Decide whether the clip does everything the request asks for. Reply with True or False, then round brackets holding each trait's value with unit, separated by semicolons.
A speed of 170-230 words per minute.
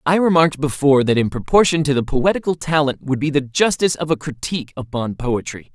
True (200 wpm)